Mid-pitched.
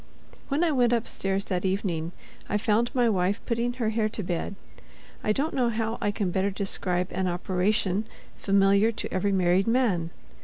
No: high, 200 Hz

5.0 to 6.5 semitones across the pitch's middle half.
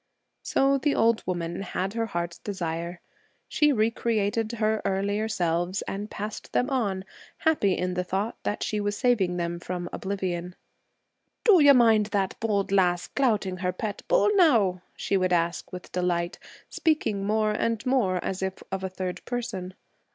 No: average, 3.8 semitones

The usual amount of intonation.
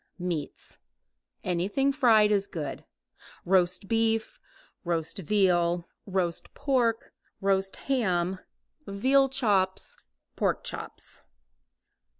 Yes: average, 4.2 semitones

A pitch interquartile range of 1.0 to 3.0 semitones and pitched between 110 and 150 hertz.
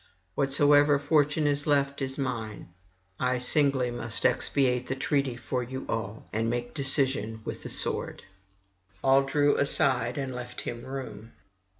Yes: narrow, 2.6 semitones; low, 135 Hz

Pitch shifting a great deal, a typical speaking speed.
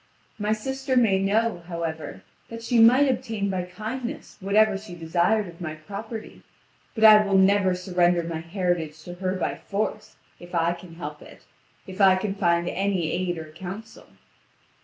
No: average, 3.8 semitones; average, 170 wpm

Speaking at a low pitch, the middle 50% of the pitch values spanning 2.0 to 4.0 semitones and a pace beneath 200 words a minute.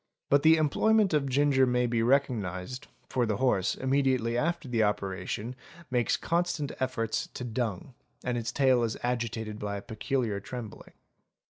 Yes: low, 125 Hz; average, 3.7 semitones; average, 150 wpm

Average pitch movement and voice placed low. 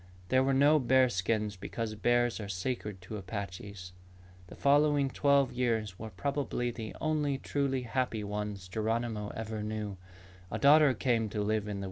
Yes: average, 4.1 semitones; low, 115 Hz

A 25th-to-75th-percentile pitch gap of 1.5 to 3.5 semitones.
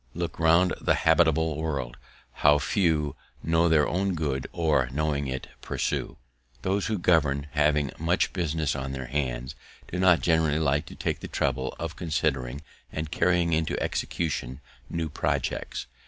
Yes: average, 2.8 semitones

